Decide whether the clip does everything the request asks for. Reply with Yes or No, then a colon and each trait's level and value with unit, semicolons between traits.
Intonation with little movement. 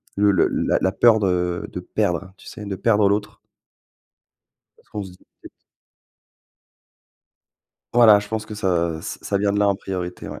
Yes: narrow, 2.2 semitones